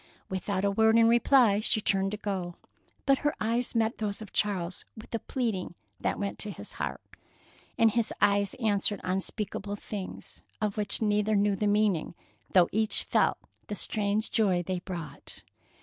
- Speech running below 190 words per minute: Yes, average, 165 wpm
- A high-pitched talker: Yes, high, 205 Hz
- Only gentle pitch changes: Yes, narrow, 2.1 semitones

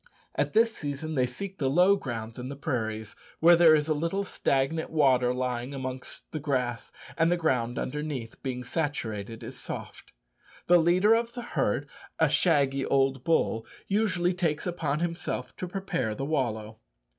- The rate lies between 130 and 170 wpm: Yes, average, 165 wpm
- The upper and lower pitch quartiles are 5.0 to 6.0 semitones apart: Yes, wide, 5.4 semitones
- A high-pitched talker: No, medium, 145 Hz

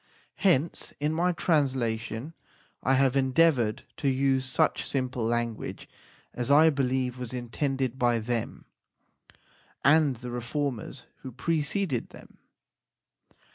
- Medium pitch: No, low, 130 Hz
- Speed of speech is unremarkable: No, slow, 115 wpm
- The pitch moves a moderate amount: Yes, average, 3.1 semitones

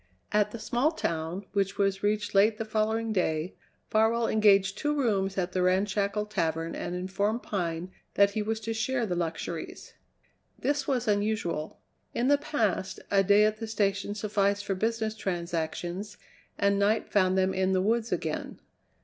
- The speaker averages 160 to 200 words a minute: Yes, average, 165 wpm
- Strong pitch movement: No, average, 2.7 semitones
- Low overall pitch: No, high, 205 Hz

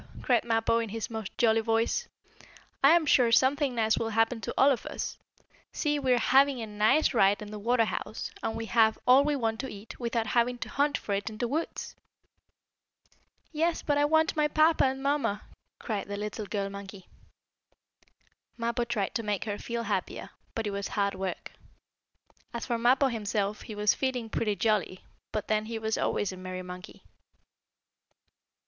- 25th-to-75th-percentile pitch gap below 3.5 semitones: No, average, 3.8 semitones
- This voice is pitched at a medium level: No, high, 225 Hz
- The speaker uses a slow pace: No, average, 185 wpm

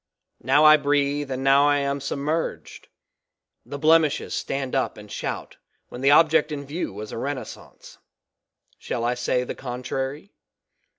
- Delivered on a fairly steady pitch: Yes, narrow, 2.3 semitones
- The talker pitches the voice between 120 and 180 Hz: Yes, medium, 140 Hz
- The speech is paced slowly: No, average, 155 wpm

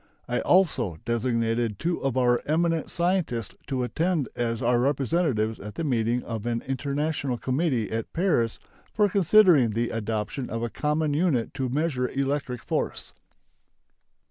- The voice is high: No, low, 130 Hz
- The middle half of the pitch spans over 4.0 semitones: Yes, average, 5.2 semitones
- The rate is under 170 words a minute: Yes, average, 145 wpm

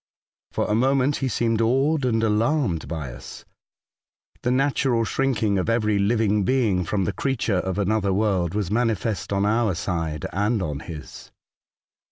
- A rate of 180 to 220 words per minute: No, average, 160 wpm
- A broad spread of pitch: No, average, 4.0 semitones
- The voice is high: No, low, 105 Hz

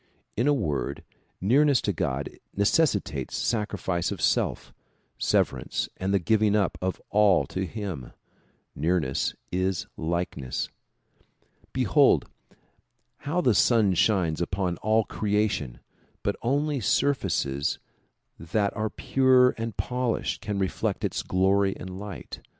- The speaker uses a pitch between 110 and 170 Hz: No, low, 100 Hz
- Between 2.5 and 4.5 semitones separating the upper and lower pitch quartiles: Yes, average, 4.2 semitones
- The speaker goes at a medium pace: No, slow, 120 wpm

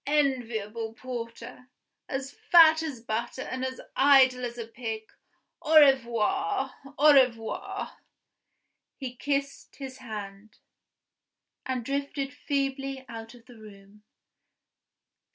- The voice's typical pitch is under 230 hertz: No, very high, 255 Hz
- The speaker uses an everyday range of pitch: Yes, average, 3.4 semitones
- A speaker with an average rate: No, slow, 105 wpm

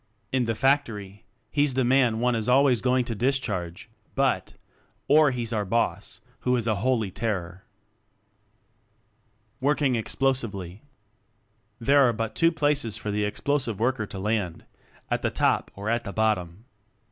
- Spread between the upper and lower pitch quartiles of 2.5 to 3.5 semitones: No, average, 4.1 semitones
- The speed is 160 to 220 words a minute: No, average, 150 wpm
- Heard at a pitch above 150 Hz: No, low, 115 Hz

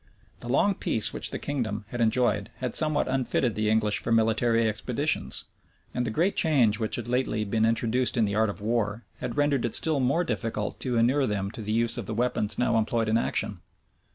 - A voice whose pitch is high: No, low, 115 Hz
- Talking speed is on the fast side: Yes, fast, 210 wpm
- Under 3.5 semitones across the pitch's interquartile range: Yes, narrow, 2.6 semitones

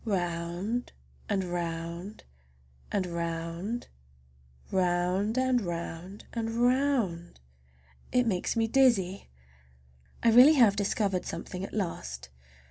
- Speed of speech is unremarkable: No, slow, 90 wpm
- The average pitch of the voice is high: No, medium, 180 Hz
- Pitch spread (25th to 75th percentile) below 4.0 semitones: No, average, 5.1 semitones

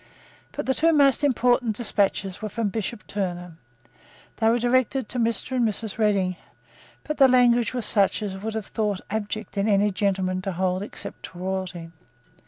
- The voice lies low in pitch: No, high, 215 Hz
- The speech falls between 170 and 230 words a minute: Yes, average, 180 wpm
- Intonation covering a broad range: No, average, 3.9 semitones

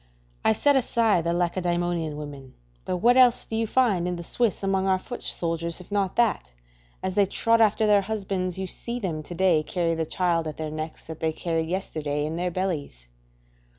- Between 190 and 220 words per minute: Yes, average, 200 wpm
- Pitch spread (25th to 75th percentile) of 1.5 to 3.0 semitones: No, average, 3.8 semitones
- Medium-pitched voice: Yes, medium, 180 Hz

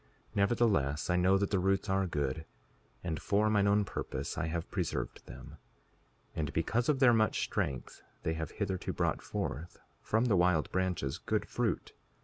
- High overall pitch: No, very low, 95 Hz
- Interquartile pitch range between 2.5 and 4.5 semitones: Yes, average, 4.2 semitones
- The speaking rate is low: No, average, 170 wpm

